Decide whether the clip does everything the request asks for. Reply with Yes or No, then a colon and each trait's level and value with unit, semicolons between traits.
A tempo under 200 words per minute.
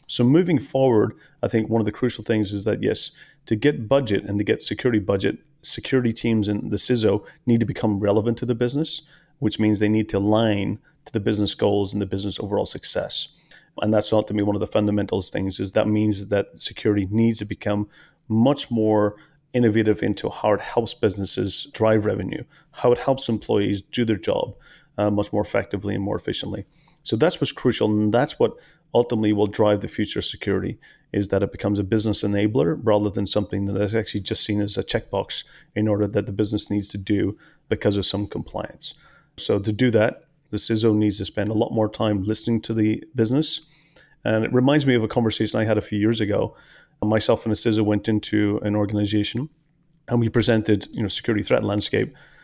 No: fast, 205 wpm